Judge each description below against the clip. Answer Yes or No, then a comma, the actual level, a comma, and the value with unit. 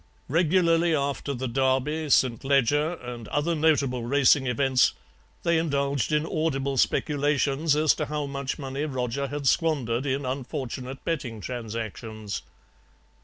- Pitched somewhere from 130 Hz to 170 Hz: Yes, medium, 140 Hz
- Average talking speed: No, slow, 125 wpm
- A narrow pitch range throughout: No, average, 3.0 semitones